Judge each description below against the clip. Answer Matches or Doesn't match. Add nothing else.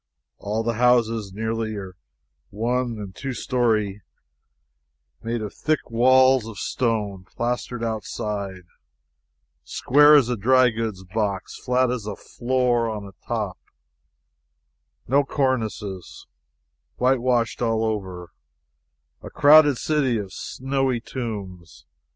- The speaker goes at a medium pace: Doesn't match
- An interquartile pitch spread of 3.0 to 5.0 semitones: Matches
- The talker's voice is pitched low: Matches